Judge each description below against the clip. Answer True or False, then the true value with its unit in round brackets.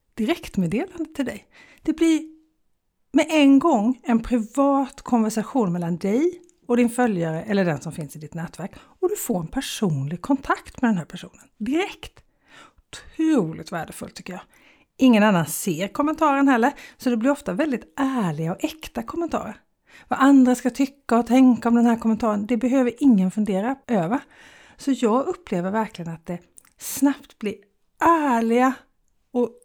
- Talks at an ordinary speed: True (155 wpm)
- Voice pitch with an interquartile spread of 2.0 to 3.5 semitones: False (5.4 semitones)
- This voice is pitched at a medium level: False (245 Hz)